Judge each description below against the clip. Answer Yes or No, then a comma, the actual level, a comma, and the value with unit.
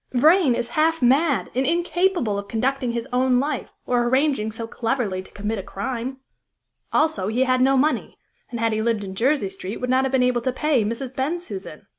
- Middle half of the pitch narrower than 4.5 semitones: Yes, average, 3.3 semitones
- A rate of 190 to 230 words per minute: Yes, average, 200 wpm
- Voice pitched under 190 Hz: No, very high, 250 Hz